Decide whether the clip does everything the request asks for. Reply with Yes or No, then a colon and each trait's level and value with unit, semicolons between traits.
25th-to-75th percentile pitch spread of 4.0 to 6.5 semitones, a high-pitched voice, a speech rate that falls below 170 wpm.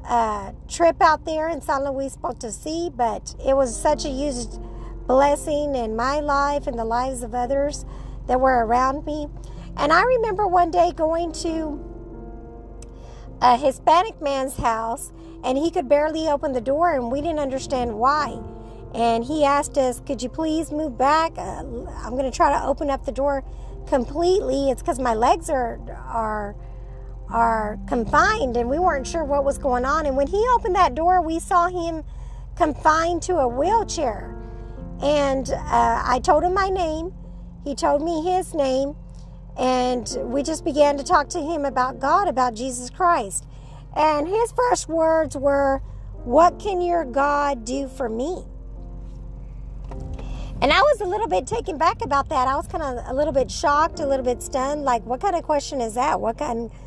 No: average, 4.6 semitones; very high, 280 Hz; average, 175 wpm